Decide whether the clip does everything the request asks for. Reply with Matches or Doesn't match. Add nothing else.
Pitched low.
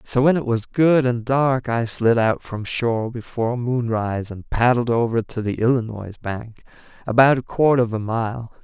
Matches